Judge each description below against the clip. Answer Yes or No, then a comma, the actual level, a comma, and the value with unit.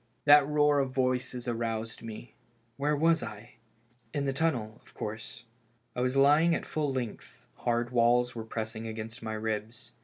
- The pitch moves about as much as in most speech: Yes, average, 3.8 semitones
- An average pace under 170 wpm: Yes, average, 160 wpm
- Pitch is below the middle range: Yes, low, 120 Hz